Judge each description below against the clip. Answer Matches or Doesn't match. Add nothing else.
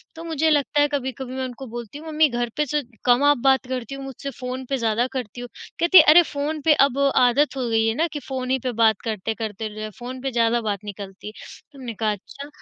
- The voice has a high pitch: Matches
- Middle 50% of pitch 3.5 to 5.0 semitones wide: Matches